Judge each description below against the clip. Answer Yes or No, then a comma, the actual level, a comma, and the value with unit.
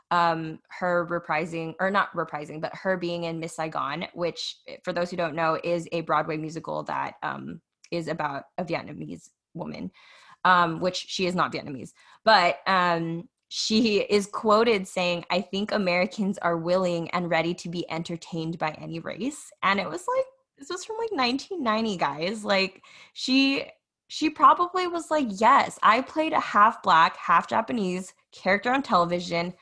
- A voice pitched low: No, medium, 180 Hz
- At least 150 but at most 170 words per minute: Yes, average, 165 wpm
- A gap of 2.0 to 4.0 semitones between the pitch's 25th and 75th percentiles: No, average, 4.6 semitones